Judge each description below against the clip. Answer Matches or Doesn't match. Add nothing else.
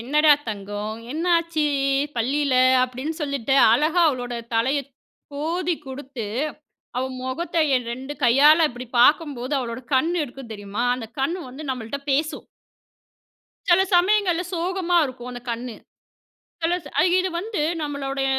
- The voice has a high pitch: Matches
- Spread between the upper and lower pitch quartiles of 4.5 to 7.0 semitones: Matches